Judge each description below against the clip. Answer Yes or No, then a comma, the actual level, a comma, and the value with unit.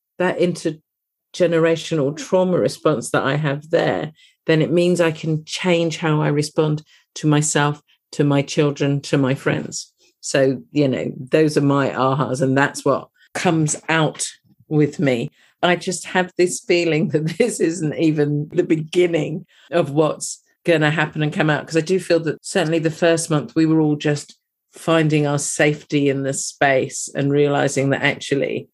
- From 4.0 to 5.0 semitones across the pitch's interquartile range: No, narrow, 2.4 semitones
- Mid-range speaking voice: Yes, medium, 155 Hz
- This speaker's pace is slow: No, average, 170 wpm